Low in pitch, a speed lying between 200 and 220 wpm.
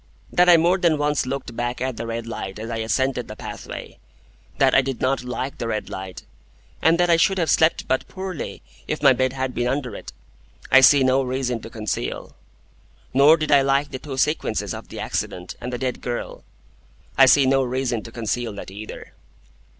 Yes: low, 130 Hz; fast, 205 wpm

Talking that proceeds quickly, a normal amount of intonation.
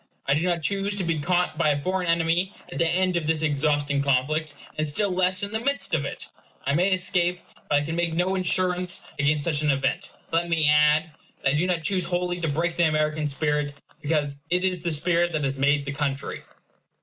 Yes: fast, 220 wpm; average, 3.4 semitones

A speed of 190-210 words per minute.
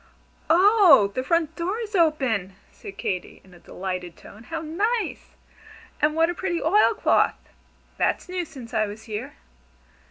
No: average, 155 wpm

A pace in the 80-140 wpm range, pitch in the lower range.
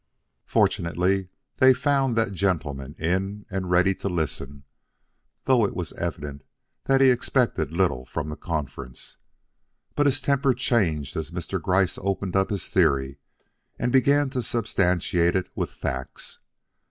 Yes: slow, 135 wpm; very low, 95 Hz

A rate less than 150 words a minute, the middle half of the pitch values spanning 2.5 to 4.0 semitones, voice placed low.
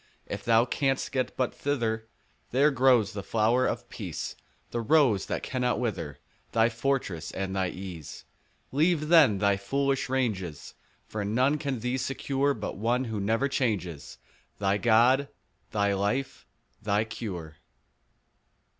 No: average, 140 wpm; average, 4.7 semitones; low, 115 Hz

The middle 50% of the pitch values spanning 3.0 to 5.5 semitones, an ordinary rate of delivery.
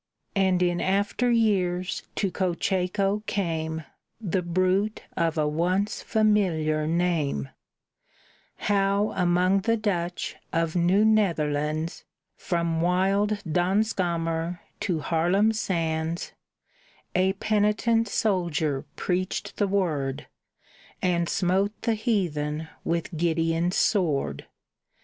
No: average, 3.5 semitones; slow, 95 wpm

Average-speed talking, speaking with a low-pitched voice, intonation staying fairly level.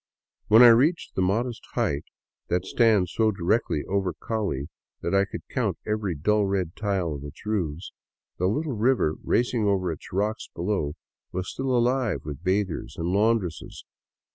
No: average, 160 wpm; low, 100 Hz; average, 4.1 semitones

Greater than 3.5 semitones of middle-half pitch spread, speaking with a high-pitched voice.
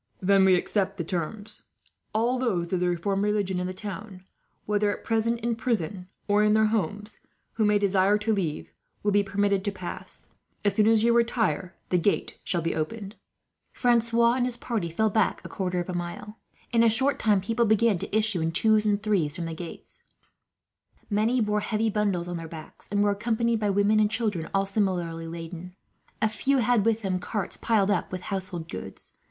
No: average, 3.2 semitones; high, 205 Hz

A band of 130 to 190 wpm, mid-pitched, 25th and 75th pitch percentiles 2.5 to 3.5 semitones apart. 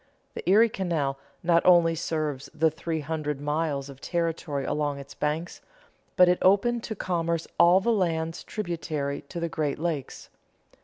Yes: average, 155 wpm; medium, 165 Hz; average, 2.9 semitones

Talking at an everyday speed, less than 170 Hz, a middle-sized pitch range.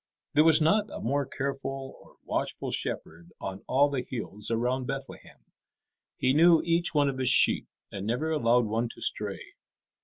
Yes: average, 165 wpm; low, 135 Hz; average, 4.3 semitones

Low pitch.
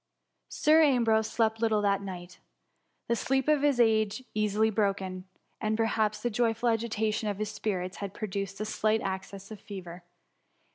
No: high, 215 Hz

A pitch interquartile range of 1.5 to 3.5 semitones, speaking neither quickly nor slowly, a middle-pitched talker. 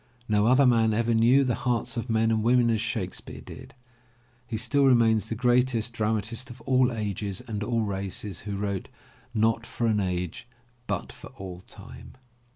No: narrow, 2.5 semitones; average, 170 wpm; low, 115 Hz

